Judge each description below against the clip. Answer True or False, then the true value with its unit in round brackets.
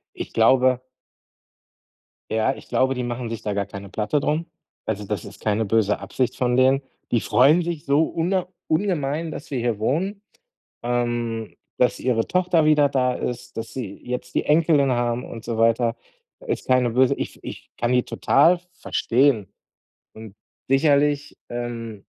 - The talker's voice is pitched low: True (125 Hz)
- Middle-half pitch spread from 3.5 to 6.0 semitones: True (4.2 semitones)